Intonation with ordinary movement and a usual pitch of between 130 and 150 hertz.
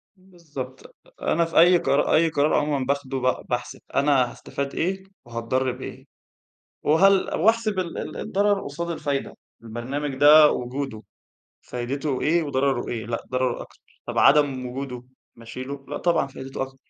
Yes: average, 3.9 semitones; medium, 140 Hz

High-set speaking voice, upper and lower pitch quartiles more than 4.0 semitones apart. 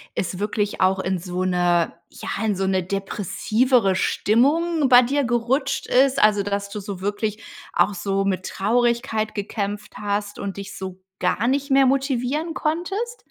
Yes: high, 210 Hz; average, 5.2 semitones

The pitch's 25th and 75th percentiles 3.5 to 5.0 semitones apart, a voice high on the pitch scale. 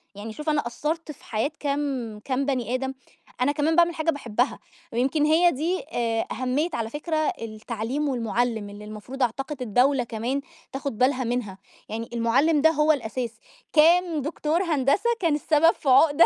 Yes: average, 4.4 semitones; very high, 270 Hz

